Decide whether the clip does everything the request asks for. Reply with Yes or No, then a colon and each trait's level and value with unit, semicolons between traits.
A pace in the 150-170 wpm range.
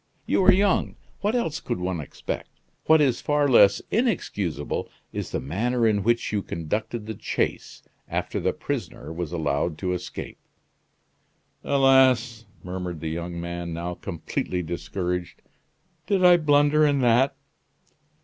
No: average, 140 wpm